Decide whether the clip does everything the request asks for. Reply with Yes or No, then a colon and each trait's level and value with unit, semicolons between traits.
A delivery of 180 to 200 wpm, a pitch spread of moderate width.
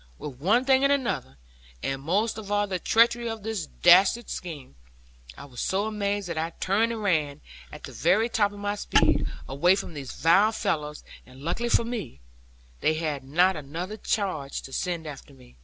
No: average, 190 wpm; wide, 6.4 semitones